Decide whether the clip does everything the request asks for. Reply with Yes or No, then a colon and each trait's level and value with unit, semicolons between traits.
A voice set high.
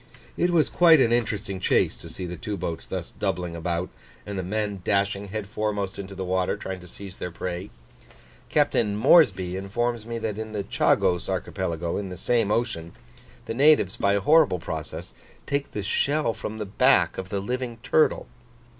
No: low, 100 Hz